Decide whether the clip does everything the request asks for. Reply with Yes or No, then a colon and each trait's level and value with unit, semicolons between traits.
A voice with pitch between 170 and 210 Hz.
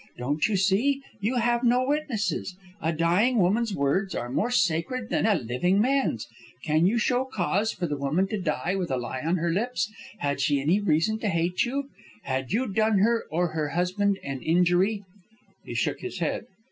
Yes: high, 190 Hz